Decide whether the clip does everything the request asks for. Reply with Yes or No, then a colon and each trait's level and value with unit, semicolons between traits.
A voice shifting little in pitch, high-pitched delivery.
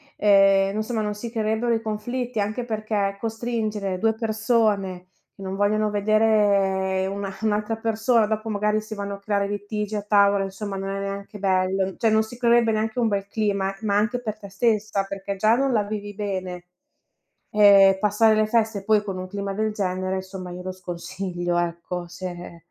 Yes: narrow, 2.0 semitones; high, 205 Hz